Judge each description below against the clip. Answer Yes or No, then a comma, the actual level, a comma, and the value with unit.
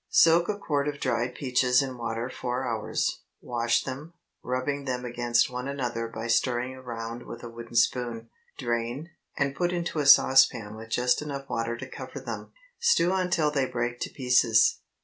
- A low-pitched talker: Yes, low, 125 Hz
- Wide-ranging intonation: No, average, 3.0 semitones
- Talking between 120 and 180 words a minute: Yes, average, 170 wpm